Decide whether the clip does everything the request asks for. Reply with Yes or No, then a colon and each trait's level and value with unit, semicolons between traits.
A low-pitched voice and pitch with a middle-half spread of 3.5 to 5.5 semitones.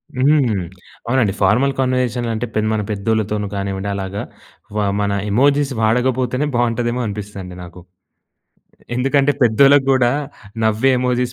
Yes: low, 120 Hz; average, 4.0 semitones